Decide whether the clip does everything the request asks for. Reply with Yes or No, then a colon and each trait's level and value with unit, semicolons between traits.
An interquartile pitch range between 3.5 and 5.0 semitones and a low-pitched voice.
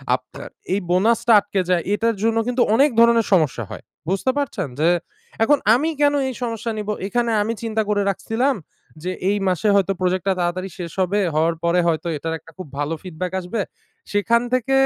No: average, 4.4 semitones; high, 205 Hz